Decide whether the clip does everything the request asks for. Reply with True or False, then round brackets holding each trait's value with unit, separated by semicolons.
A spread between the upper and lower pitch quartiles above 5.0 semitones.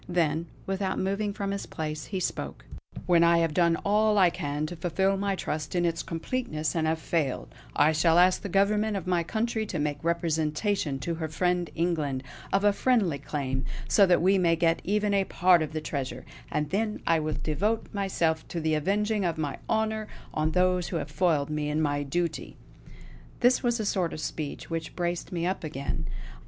False (4.0 semitones)